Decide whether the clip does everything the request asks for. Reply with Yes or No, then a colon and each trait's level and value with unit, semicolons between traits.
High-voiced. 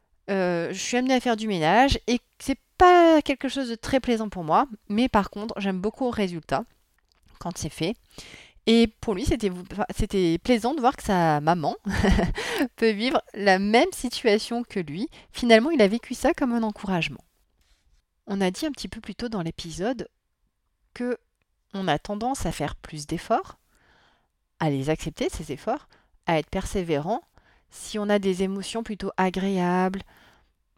Yes: high, 205 Hz